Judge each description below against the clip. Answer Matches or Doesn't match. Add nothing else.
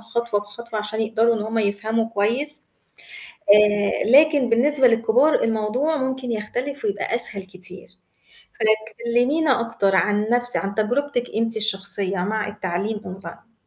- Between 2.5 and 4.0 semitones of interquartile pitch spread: Matches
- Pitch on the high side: Matches